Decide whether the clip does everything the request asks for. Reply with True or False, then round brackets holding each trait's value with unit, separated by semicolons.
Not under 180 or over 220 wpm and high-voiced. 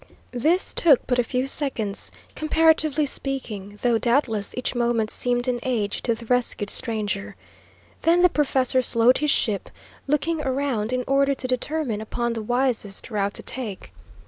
False (155 wpm; 250 Hz)